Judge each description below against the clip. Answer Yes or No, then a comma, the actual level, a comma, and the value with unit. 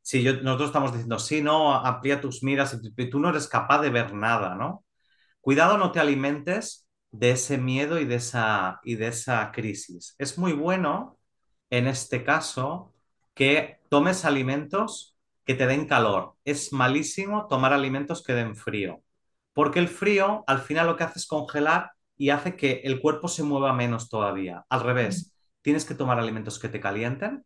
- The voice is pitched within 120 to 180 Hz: Yes, low, 135 Hz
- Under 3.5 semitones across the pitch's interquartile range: No, average, 4.3 semitones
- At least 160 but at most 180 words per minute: Yes, average, 175 wpm